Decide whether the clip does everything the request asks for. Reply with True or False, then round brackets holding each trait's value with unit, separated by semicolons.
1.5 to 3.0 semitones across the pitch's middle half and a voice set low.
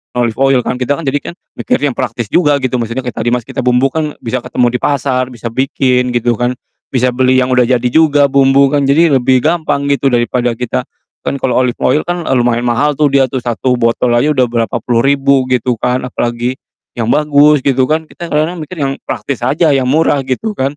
True (2.6 semitones; 130 Hz)